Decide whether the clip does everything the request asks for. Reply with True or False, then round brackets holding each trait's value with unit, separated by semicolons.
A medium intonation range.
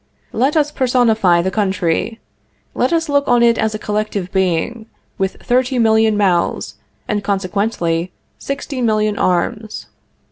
True (4.1 semitones)